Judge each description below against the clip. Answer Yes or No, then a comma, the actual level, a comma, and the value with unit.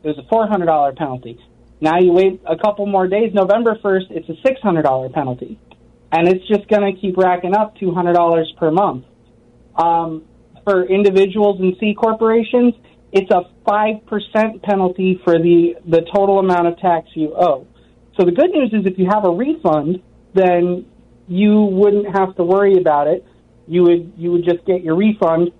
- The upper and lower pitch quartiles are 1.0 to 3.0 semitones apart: No, average, 3.5 semitones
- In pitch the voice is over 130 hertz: Yes, medium, 185 Hz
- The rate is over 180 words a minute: Yes, average, 190 wpm